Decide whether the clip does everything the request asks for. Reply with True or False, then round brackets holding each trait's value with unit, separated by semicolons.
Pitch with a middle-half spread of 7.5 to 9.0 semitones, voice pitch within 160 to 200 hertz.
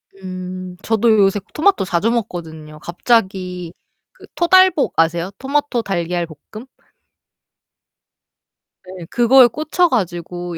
False (5.6 semitones; 190 Hz)